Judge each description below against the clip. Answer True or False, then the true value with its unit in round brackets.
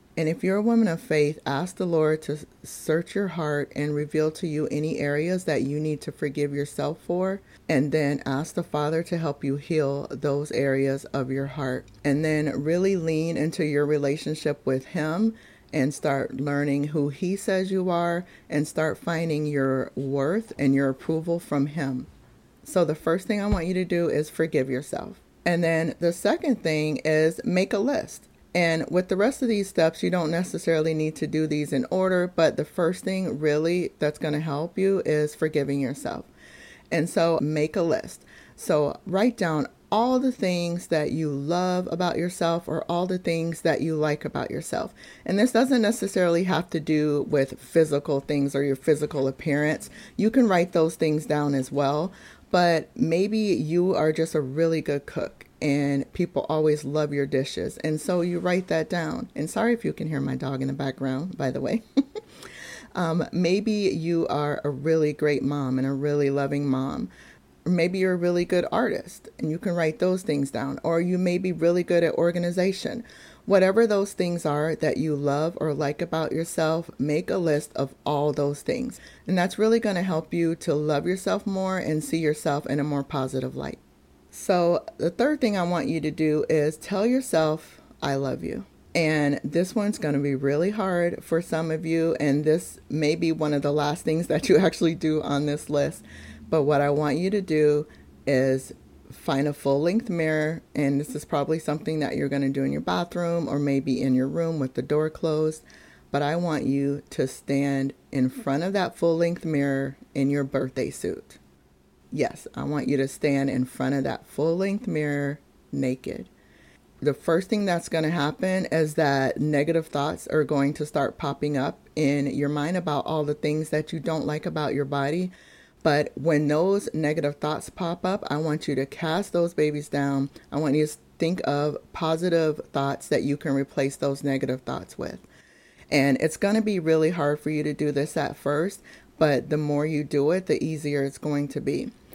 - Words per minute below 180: False (195 wpm)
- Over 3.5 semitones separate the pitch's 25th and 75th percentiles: False (3.2 semitones)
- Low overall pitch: False (155 Hz)